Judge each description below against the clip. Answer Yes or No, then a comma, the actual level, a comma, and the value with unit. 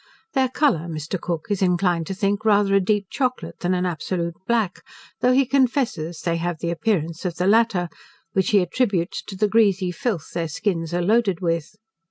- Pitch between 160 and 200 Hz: Yes, medium, 185 Hz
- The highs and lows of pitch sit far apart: No, average, 4.2 semitones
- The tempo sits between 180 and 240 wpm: Yes, average, 190 wpm